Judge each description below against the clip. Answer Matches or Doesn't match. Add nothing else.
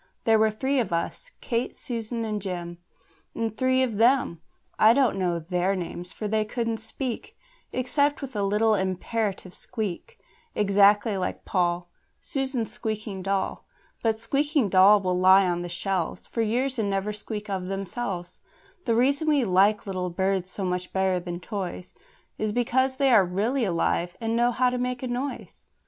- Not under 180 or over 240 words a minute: Doesn't match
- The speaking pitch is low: Doesn't match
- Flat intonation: Doesn't match